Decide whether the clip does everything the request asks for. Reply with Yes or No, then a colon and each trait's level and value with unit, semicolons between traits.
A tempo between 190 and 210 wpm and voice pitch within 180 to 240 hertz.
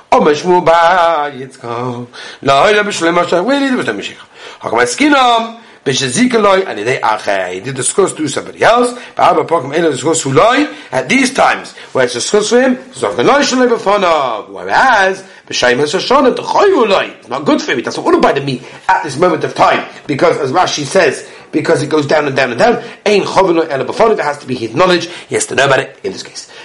Yes: fast, 205 wpm; high, 190 Hz